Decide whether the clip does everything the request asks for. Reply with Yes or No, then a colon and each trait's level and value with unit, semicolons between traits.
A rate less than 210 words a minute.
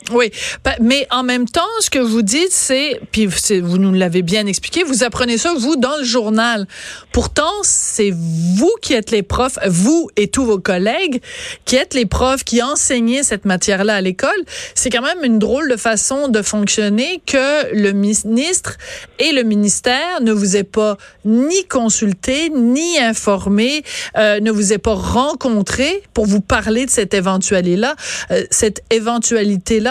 Yes: average, 170 wpm